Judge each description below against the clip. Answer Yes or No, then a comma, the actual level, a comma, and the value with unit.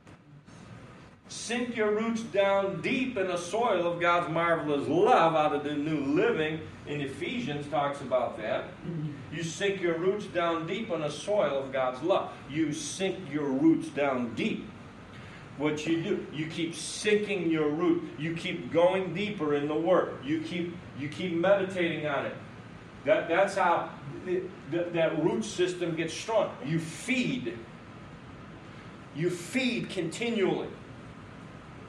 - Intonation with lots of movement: No, average, 4.0 semitones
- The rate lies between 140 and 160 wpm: Yes, average, 145 wpm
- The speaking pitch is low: No, medium, 170 Hz